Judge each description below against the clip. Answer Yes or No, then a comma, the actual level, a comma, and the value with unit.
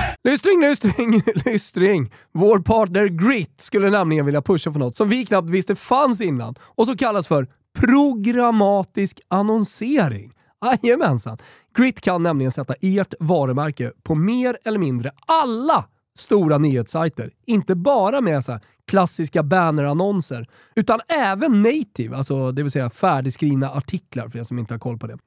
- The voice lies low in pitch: No, medium, 185 Hz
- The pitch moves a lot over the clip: Yes, wide, 8.2 semitones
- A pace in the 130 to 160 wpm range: Yes, average, 145 wpm